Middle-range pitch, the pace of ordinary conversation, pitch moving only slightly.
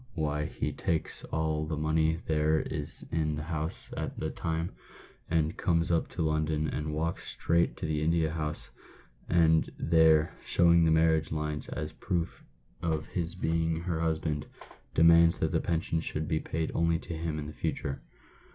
No: very low, 80 Hz; average, 165 wpm; narrow, 1.2 semitones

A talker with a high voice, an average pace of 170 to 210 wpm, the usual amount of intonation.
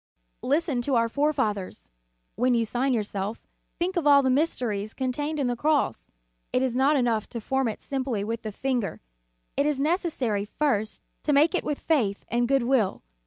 Yes: very high, 255 Hz; average, 190 wpm; average, 4.3 semitones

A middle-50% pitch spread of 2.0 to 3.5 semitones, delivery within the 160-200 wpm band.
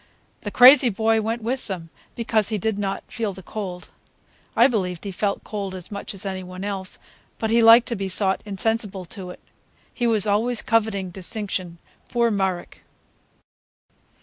Yes: average, 3.0 semitones; average, 170 wpm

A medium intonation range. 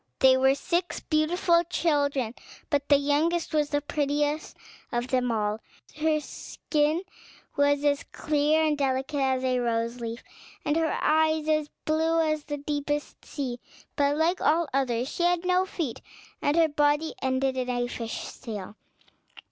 Yes: average, 3.1 semitones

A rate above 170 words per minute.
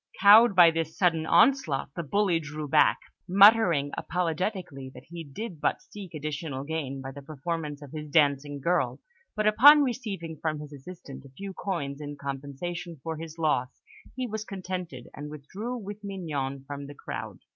No: average, 165 wpm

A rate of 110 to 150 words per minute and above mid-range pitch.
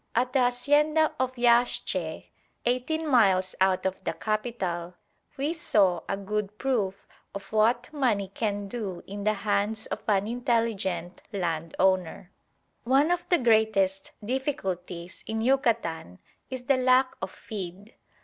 Yes: slow, 135 wpm; high, 215 Hz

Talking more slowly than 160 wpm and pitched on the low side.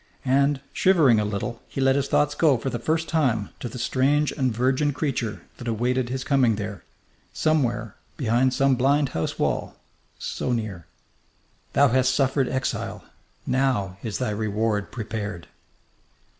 Yes: average, 150 wpm; low, 130 Hz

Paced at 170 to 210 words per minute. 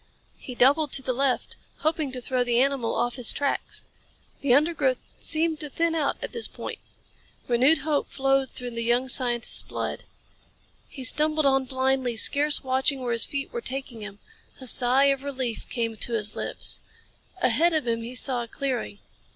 Yes: average, 175 wpm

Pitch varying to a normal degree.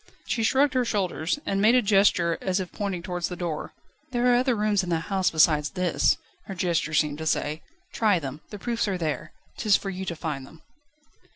Yes: average, 4.4 semitones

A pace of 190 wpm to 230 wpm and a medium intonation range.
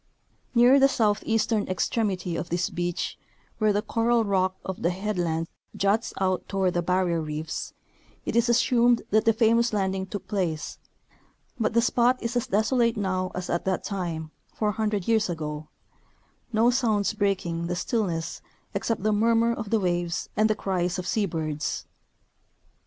No: average, 165 wpm; average, 4.3 semitones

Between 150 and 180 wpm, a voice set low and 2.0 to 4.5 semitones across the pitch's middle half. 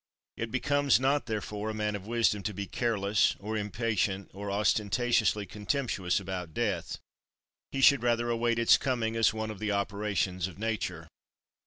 Yes: average, 160 wpm; low, 105 Hz; average, 2.8 semitones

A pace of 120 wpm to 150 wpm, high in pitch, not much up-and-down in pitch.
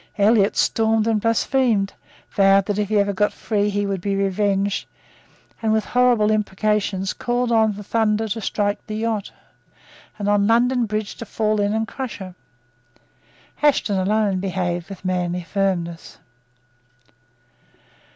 Yes: average, 140 wpm; high, 205 Hz; narrow, 2.1 semitones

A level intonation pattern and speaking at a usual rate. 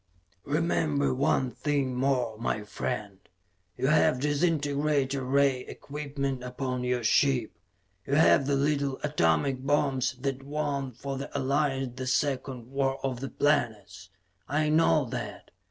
No: narrow, 2.2 semitones; slow, 130 wpm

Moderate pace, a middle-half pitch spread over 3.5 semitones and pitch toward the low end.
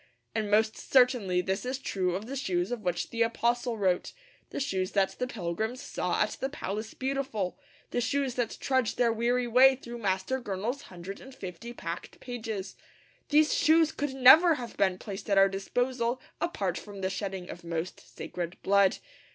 No: average, 175 wpm; average, 4.9 semitones; high, 225 Hz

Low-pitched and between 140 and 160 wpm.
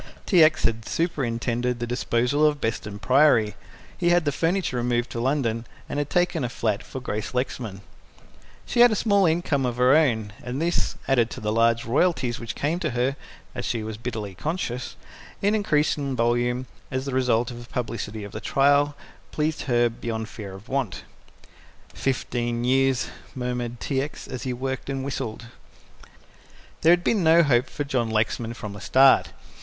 No: low, 125 Hz; average, 175 wpm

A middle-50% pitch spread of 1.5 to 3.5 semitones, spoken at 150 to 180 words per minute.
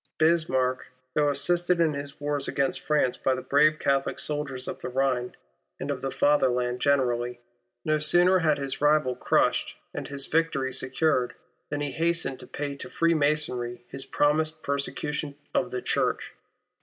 Yes: average, 2.8 semitones; average, 155 wpm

